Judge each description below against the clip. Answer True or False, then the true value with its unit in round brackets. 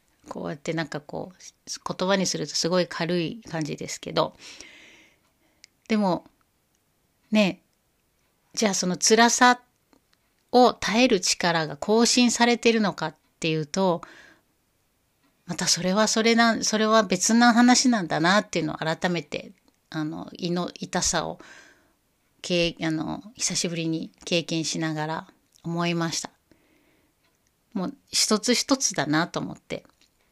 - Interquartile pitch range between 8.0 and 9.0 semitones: False (5.6 semitones)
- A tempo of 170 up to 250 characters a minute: True (240 characters per minute)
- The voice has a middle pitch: True (180 Hz)